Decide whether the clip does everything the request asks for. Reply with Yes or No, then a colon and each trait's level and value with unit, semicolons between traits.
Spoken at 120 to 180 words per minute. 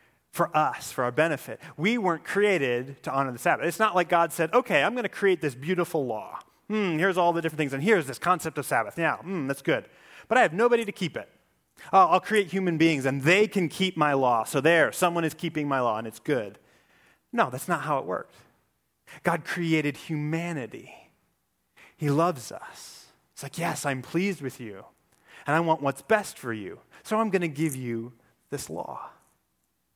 No: fast, 205 wpm